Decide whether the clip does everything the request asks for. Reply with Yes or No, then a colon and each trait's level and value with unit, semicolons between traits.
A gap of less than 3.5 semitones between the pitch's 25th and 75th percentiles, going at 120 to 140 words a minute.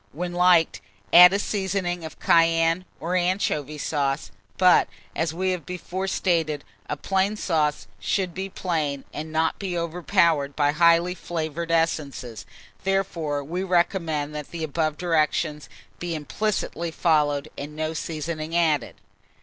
Yes: average, 2.8 semitones; slow, 135 wpm